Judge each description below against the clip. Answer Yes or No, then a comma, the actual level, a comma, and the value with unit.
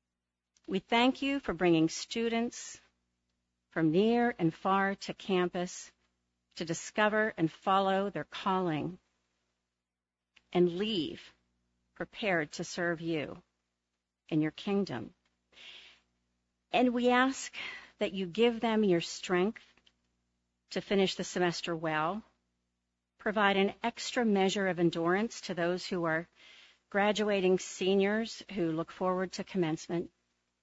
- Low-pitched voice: No, medium, 175 Hz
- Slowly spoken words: Yes, slow, 115 wpm